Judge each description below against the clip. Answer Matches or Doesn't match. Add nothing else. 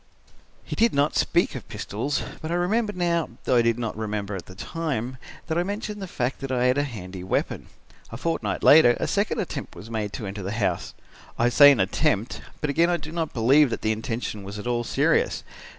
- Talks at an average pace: Doesn't match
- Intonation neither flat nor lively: Doesn't match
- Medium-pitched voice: Doesn't match